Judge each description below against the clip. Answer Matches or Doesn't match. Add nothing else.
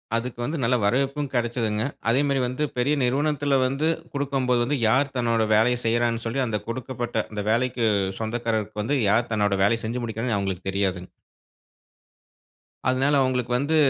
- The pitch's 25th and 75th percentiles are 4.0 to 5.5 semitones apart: Doesn't match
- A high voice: Doesn't match